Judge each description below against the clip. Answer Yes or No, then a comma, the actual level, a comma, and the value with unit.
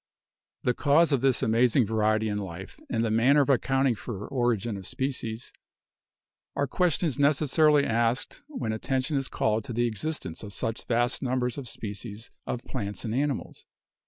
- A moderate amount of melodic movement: Yes, average, 3.9 semitones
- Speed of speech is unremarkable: Yes, average, 165 wpm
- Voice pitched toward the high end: No, low, 120 Hz